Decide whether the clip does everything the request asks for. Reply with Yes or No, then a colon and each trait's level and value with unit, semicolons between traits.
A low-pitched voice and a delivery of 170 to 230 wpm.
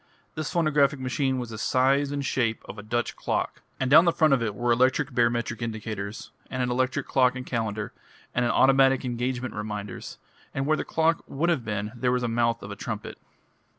Yes: low, 125 Hz; average, 195 wpm